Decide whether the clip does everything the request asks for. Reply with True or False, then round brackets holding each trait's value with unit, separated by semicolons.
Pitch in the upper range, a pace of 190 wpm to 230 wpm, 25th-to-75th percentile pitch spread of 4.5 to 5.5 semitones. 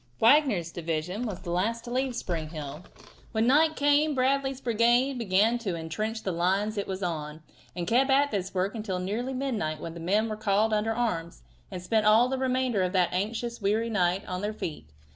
True (215 Hz; 200 wpm; 5.1 semitones)